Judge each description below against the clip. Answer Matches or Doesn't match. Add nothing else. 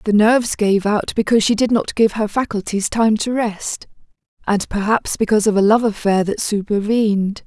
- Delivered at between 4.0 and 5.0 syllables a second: Doesn't match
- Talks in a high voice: Matches